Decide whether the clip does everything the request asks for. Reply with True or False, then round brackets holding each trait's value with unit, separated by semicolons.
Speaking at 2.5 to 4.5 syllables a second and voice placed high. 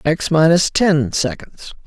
False (3.6 syllables/s; 155 Hz)